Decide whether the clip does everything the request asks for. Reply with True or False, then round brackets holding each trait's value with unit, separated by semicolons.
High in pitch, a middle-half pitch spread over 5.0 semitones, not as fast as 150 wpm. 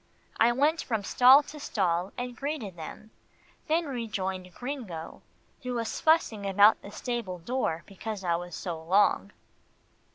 True (215 Hz; 5.4 semitones; 140 wpm)